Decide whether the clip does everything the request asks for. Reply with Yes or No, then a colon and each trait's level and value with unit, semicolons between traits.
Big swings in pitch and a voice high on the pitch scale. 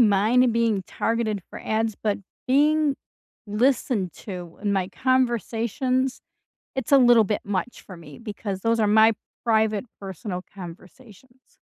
No: average, 3.8 semitones; high, 220 Hz